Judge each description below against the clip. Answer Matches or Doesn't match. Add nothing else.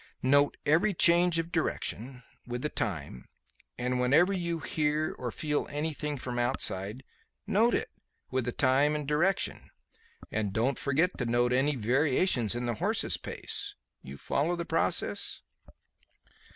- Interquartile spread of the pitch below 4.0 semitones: Doesn't match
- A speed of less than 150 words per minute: Matches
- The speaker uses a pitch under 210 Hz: Matches